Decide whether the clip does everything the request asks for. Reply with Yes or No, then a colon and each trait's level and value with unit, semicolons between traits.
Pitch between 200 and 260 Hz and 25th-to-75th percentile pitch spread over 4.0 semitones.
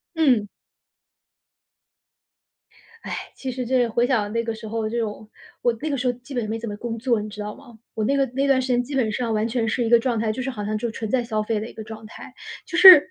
No: high, 230 Hz; average, 2.7 semitones